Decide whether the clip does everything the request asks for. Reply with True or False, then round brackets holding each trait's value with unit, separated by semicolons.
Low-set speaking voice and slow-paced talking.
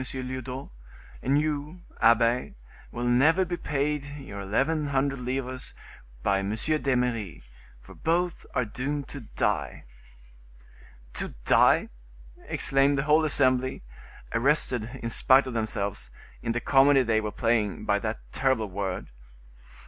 True (130 Hz; 125 wpm)